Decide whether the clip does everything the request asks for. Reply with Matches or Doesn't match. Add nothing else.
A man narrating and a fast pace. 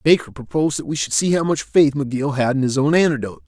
Matches